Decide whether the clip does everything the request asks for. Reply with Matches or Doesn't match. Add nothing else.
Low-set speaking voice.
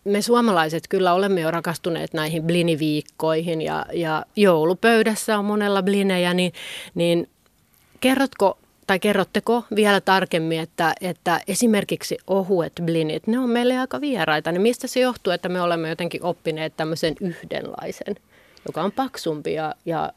Doesn't match